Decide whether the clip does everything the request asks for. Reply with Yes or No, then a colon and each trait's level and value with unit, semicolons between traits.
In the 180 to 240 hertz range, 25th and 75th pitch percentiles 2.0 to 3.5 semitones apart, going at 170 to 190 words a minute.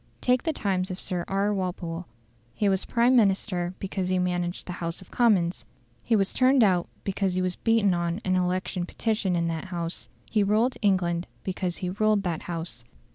Yes: medium, 185 Hz; average, 2.8 semitones; average, 185 wpm